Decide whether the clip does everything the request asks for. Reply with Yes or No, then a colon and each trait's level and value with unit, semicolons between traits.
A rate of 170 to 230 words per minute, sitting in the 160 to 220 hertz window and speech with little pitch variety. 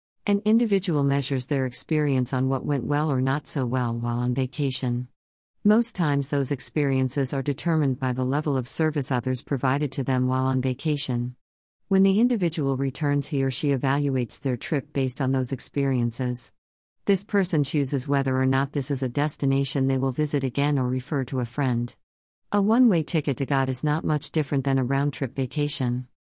No: average, 185 wpm; low, 135 Hz; narrow, 2.3 semitones